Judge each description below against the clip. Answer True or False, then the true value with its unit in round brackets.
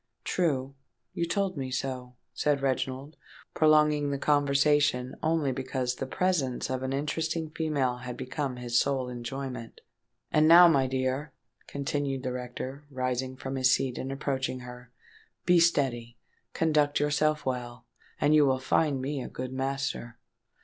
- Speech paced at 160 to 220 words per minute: False (135 wpm)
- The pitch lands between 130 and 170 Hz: True (135 Hz)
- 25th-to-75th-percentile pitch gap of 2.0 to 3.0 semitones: True (2.5 semitones)